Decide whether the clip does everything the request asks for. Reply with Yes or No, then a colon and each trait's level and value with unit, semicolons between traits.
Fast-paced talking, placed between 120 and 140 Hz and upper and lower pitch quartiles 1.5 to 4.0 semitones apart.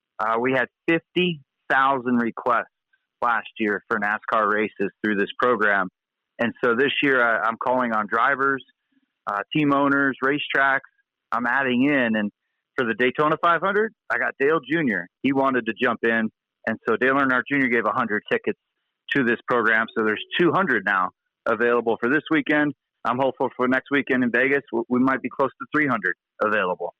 No: average, 170 wpm; low, 135 Hz; average, 3.6 semitones